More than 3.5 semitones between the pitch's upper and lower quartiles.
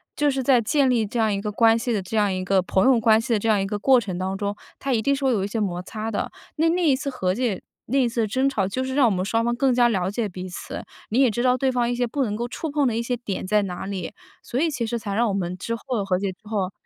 Yes: average, 4.2 semitones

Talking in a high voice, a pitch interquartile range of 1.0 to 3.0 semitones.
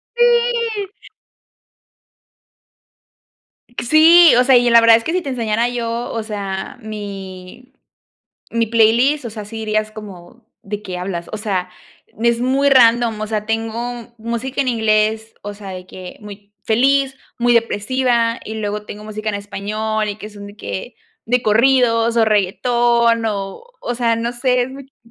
Yes: high, 225 Hz; average, 2.7 semitones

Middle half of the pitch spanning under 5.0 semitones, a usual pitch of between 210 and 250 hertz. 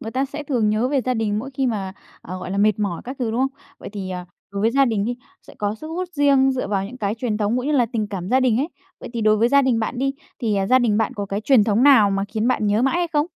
Yes: average, 4.3 semitones; high, 230 Hz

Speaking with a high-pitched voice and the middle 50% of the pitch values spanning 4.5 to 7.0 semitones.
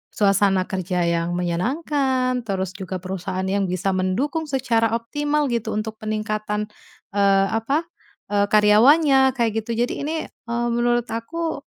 Yes: high, 215 Hz; average, 4.9 semitones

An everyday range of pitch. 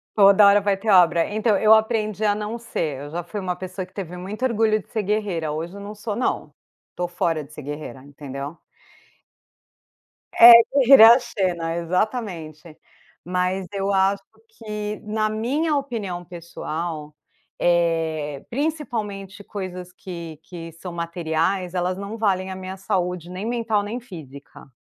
Yes: average, 4.0 semitones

